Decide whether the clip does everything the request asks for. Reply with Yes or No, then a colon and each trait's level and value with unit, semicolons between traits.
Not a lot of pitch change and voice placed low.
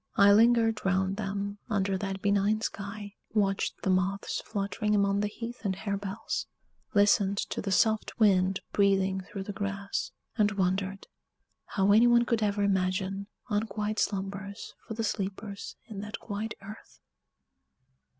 No: narrow, 1.4 semitones; high, 200 Hz